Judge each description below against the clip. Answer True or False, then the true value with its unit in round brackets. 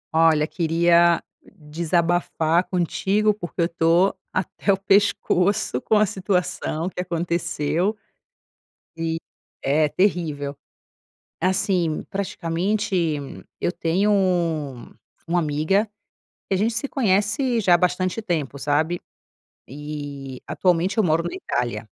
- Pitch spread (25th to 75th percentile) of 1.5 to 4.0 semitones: True (3.4 semitones)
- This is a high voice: False (175 Hz)